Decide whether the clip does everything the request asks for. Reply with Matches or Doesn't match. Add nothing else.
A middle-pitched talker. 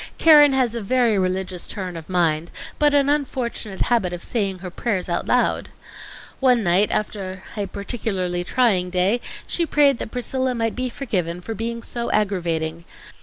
Doesn't match